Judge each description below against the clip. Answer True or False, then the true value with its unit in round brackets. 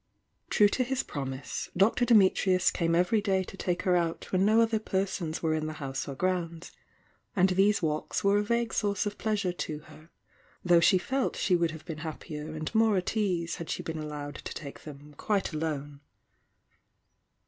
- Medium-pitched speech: True (180 Hz)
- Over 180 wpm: True (190 wpm)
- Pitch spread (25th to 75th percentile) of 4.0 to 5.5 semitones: True (4.6 semitones)